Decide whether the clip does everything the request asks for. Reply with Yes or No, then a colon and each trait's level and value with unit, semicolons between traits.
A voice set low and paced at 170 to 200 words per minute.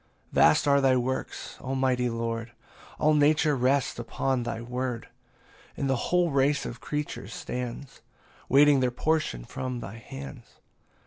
No: low, 130 Hz; average, 150 wpm